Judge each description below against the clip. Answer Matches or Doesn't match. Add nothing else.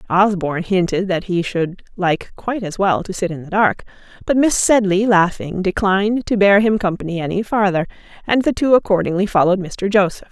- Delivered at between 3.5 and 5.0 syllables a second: Doesn't match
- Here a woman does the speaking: Matches